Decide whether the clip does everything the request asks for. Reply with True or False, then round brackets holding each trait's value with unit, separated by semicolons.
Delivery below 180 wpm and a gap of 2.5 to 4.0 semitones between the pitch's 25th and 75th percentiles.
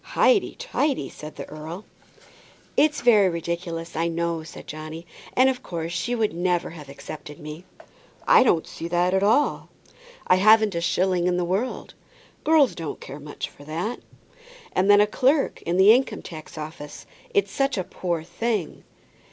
False (170 wpm; 5.0 semitones)